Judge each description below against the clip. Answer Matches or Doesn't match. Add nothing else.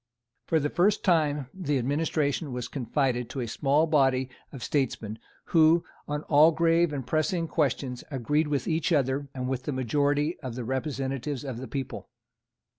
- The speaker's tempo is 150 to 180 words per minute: Matches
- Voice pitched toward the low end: Doesn't match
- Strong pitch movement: Doesn't match